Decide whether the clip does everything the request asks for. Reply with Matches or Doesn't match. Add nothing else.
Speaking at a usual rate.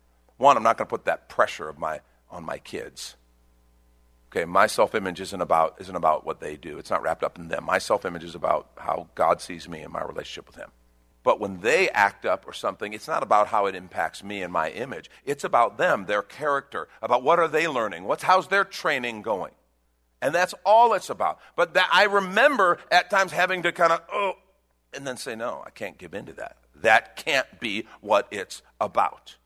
Doesn't match